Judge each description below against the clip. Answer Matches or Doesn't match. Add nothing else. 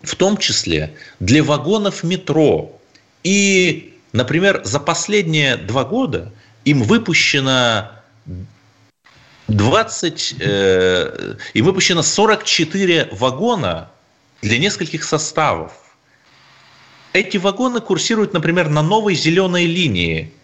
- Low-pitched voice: Doesn't match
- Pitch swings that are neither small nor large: Doesn't match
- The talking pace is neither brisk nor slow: Doesn't match